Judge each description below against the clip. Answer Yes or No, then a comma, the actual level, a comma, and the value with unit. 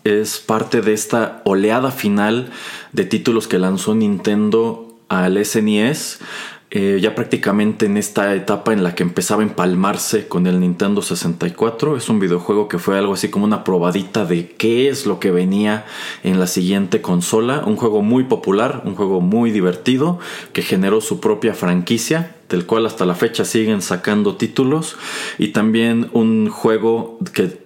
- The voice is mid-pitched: No, low, 105 Hz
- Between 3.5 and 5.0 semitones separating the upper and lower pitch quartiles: No, average, 3.0 semitones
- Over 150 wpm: Yes, average, 165 wpm